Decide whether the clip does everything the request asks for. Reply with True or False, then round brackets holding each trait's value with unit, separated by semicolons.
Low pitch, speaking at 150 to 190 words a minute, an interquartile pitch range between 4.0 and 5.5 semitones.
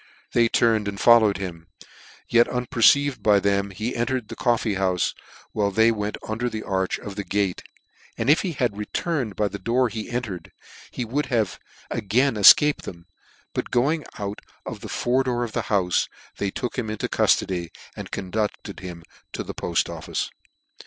False (110 Hz; 175 wpm; 3.5 semitones)